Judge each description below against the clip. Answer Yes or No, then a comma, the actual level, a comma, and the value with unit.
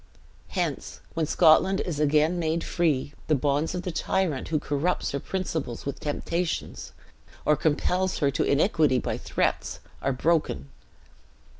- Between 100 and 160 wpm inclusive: Yes, average, 140 wpm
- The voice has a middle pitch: Yes, medium, 155 Hz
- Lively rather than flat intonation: No, average, 3.5 semitones